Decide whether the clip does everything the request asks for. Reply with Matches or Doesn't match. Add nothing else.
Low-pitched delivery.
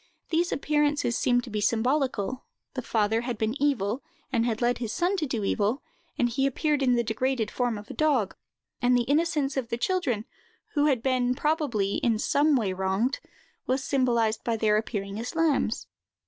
Doesn't match